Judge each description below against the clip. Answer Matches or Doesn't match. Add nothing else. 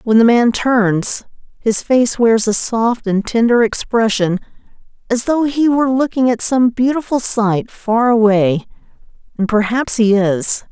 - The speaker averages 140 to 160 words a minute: Matches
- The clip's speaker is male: Doesn't match